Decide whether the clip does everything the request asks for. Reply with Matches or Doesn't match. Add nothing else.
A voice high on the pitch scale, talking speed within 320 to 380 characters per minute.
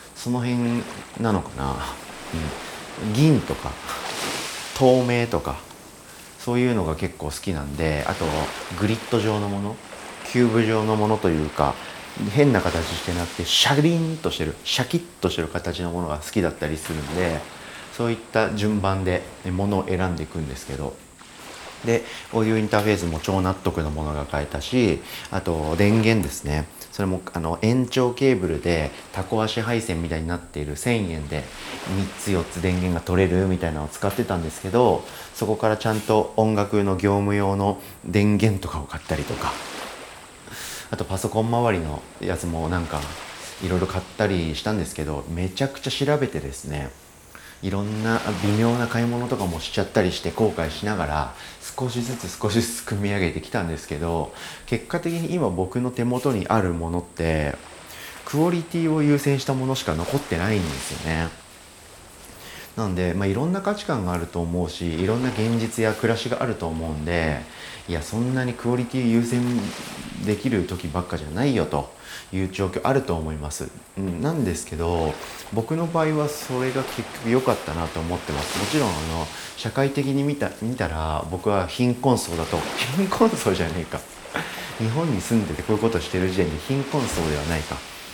Doesn't match